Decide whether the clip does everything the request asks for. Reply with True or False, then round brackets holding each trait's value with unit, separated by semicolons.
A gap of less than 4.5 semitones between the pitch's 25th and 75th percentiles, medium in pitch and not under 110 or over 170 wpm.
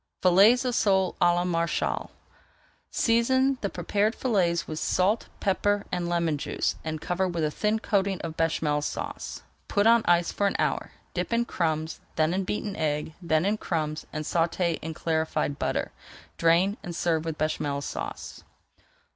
True (4.1 semitones; 175 Hz; 165 wpm)